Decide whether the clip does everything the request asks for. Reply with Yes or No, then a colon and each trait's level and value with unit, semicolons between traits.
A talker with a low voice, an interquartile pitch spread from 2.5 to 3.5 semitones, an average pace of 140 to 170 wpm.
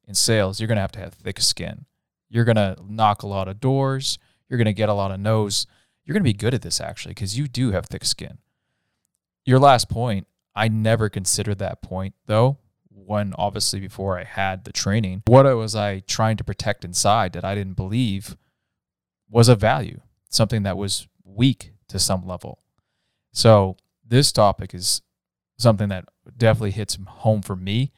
No: low, 105 Hz; average, 3.0 semitones; average, 180 wpm